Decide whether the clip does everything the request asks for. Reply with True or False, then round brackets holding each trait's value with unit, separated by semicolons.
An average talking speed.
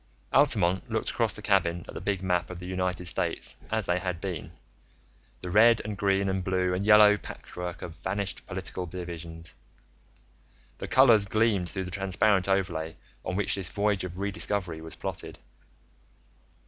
True (165 wpm)